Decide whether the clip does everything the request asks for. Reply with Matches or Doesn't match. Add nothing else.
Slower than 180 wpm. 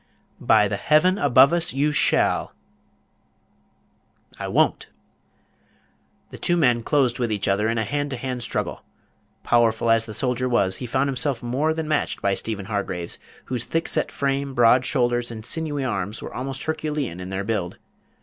Matches